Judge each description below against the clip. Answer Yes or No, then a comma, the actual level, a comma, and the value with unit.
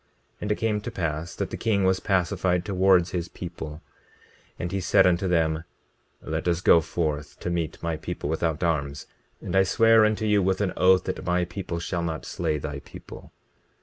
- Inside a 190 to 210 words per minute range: Yes, average, 195 wpm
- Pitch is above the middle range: No, very low, 90 Hz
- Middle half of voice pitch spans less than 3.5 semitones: Yes, average, 2.9 semitones